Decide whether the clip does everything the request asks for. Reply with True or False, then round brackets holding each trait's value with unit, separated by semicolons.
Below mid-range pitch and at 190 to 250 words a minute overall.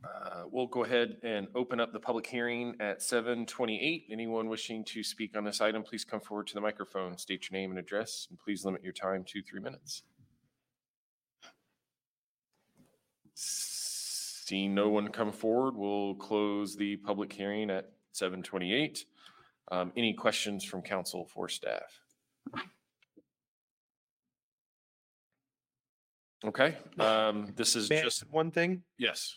False (110 Hz; 140 wpm)